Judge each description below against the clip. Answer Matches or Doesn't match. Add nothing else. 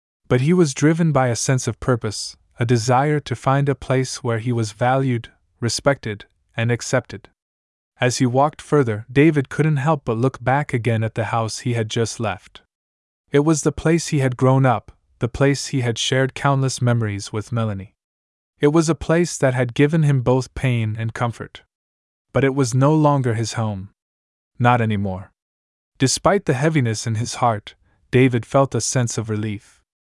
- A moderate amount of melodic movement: Matches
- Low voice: Matches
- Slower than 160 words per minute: Doesn't match